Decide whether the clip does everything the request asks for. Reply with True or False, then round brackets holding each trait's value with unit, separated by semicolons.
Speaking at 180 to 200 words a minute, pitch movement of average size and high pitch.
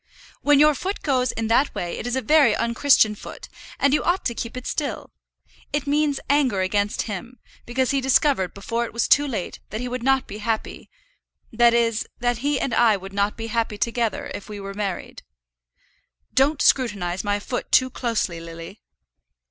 True (190 wpm; 4.5 semitones; 235 Hz)